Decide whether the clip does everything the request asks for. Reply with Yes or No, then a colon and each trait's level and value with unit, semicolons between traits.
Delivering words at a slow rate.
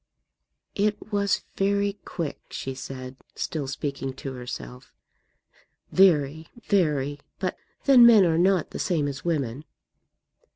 Yes: slow, 120 wpm